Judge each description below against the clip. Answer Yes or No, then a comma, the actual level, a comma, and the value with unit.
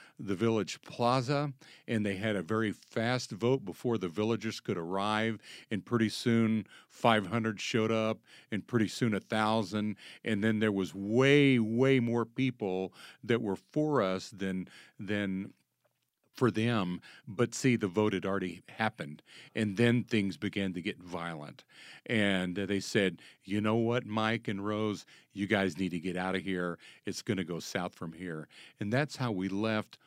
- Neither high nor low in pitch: No, low, 110 Hz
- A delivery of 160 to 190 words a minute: Yes, average, 170 wpm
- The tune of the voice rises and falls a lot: No, average, 3.2 semitones